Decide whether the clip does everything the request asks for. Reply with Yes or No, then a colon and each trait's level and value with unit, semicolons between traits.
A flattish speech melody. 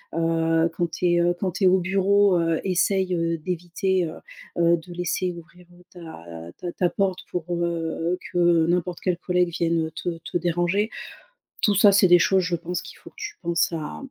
Yes: narrow, 1.6 semitones